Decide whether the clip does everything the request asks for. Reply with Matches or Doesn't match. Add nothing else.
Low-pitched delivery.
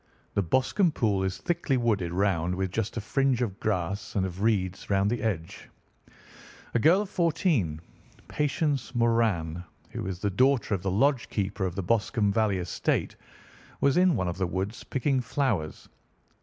Matches